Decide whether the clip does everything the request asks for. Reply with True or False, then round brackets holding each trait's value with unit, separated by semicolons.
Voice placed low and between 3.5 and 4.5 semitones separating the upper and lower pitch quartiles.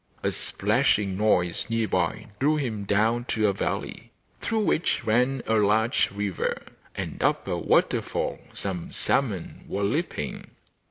True (110 Hz; 3.8 semitones)